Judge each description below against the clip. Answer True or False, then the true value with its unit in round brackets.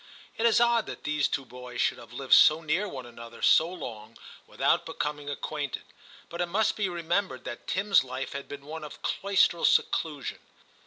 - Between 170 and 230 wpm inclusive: True (180 wpm)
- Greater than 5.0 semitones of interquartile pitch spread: True (5.4 semitones)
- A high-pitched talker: False (150 Hz)